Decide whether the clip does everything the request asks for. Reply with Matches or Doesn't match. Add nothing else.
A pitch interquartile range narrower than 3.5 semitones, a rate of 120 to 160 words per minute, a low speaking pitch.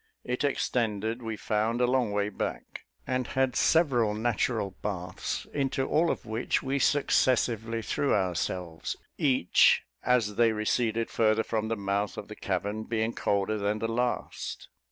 Matches